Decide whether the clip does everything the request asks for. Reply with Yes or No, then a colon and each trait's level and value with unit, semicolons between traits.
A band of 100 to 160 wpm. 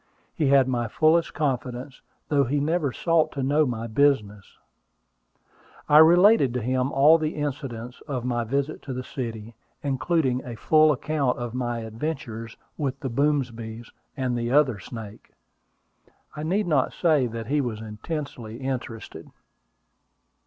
Yes: average, 145 wpm